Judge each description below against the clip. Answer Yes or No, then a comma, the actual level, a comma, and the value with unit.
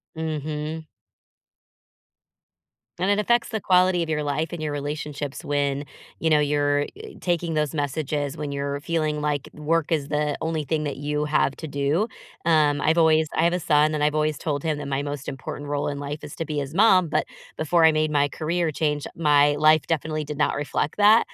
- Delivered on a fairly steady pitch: Yes, narrow, 1.8 semitones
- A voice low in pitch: No, medium, 150 Hz